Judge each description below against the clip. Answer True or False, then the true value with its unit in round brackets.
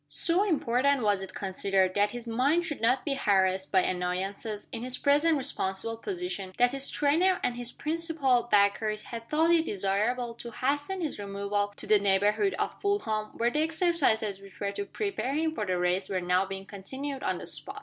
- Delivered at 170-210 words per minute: True (190 wpm)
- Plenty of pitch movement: True (6.7 semitones)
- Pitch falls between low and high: False (230 Hz)